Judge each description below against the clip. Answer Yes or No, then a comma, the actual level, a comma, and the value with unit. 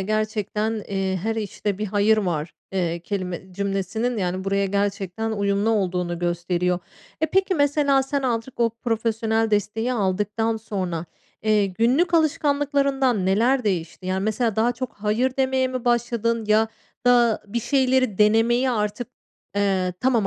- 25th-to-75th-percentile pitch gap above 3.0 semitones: Yes, average, 3.8 semitones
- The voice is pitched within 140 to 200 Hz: No, high, 215 Hz